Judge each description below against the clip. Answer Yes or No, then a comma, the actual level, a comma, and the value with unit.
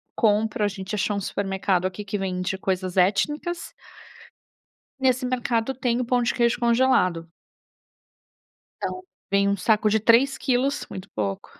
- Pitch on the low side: No, high, 210 Hz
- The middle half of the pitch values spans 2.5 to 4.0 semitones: No, average, 4.4 semitones